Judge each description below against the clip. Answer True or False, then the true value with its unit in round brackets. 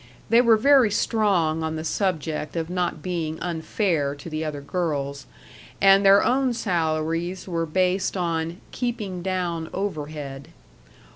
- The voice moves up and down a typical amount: True (3.7 semitones)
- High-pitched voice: False (170 Hz)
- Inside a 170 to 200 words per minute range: False (135 wpm)